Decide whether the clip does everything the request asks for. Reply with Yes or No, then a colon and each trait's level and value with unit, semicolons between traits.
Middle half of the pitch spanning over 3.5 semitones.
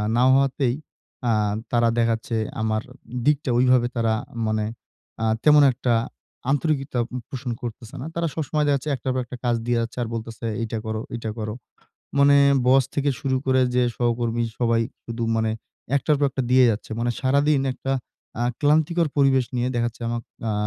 No: average, 3.0 semitones